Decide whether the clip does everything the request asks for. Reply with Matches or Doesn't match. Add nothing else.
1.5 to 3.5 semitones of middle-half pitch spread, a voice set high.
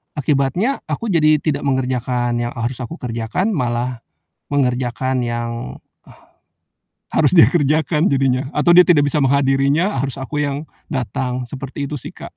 Doesn't match